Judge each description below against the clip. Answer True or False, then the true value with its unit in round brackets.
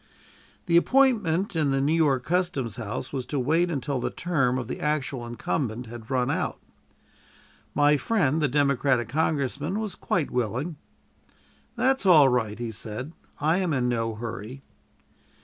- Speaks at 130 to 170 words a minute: True (150 wpm)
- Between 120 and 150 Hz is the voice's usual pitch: True (140 Hz)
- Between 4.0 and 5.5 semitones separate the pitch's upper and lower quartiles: True (5.0 semitones)